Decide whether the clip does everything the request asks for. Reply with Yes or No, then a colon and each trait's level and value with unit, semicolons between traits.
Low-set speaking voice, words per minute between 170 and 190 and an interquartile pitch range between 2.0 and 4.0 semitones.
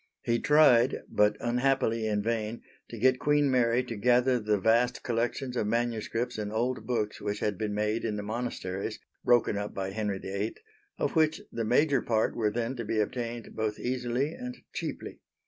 Yes: low, 115 Hz; average, 180 wpm; average, 2.7 semitones